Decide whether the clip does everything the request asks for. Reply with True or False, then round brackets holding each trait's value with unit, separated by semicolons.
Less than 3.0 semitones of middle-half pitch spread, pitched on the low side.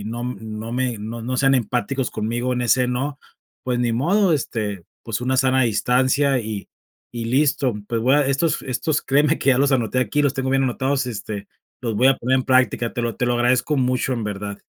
True (2.6 semitones; 125 Hz)